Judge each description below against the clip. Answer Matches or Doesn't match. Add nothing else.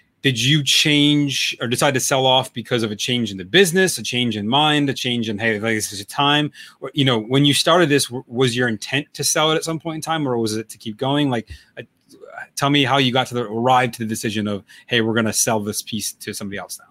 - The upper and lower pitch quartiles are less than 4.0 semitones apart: Doesn't match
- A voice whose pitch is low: Matches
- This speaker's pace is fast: Matches